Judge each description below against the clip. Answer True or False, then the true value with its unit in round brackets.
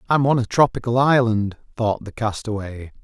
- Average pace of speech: True (160 wpm)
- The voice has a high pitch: False (115 Hz)